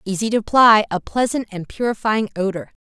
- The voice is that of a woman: Yes, female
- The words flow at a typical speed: Yes, average, 170 wpm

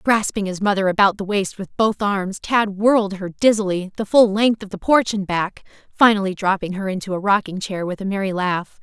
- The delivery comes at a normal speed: No, fast, 215 wpm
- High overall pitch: Yes, high, 200 Hz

